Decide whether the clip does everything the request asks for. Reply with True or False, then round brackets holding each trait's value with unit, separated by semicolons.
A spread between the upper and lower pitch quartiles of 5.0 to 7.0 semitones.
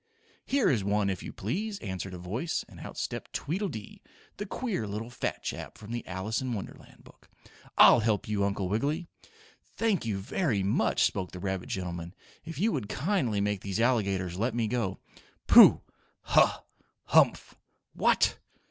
True (5.5 semitones)